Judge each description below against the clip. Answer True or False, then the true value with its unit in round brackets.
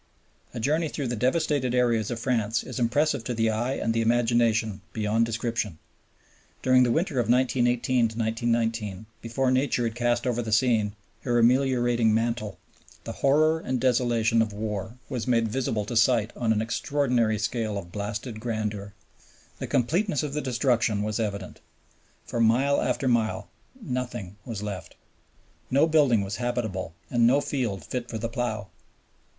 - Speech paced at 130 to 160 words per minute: True (155 wpm)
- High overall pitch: False (115 Hz)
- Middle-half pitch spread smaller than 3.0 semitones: True (2.6 semitones)